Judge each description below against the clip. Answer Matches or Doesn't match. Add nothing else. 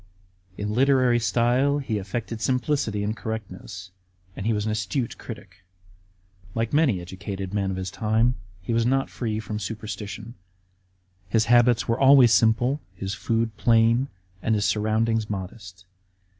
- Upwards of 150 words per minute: Doesn't match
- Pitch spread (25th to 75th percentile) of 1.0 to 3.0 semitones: Matches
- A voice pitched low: Matches